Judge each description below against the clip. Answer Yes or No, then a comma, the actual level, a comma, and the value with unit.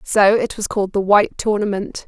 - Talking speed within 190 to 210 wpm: Yes, average, 200 wpm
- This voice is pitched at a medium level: No, high, 205 Hz